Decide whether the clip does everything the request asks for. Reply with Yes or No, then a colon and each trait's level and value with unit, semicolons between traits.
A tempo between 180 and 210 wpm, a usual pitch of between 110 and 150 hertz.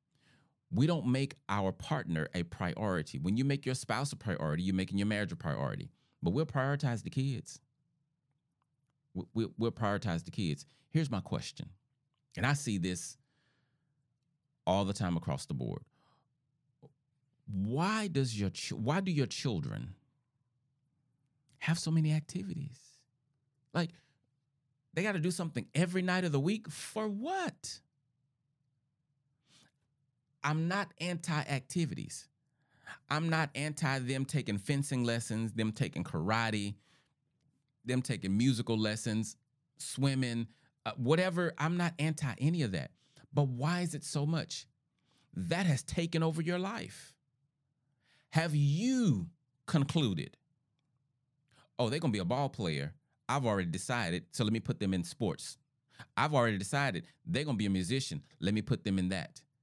No: average, 140 wpm; medium, 140 Hz